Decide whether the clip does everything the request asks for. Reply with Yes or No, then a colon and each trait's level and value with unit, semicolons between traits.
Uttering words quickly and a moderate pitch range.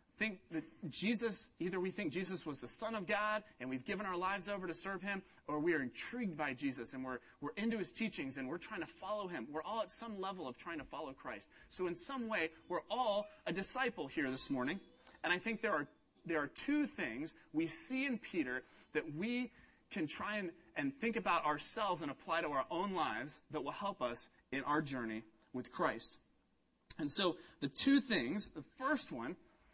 No: fast, 210 wpm; wide, 6.8 semitones